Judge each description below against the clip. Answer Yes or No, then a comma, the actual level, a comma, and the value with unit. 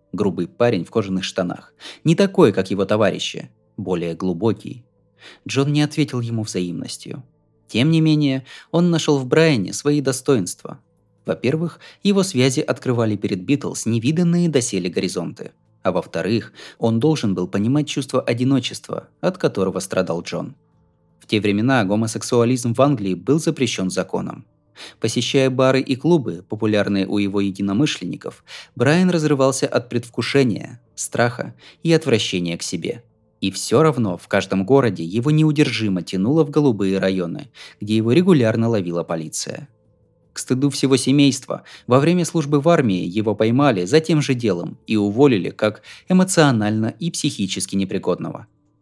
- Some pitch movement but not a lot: No, wide, 6.4 semitones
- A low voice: Yes, low, 120 Hz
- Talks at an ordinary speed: Yes, average, 140 wpm